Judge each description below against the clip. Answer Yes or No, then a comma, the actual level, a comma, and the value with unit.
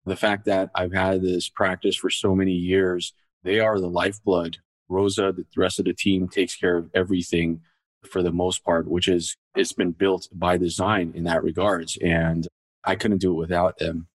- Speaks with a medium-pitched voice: No, very low, 90 Hz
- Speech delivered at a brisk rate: No, average, 195 wpm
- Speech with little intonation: Yes, narrow, 1.6 semitones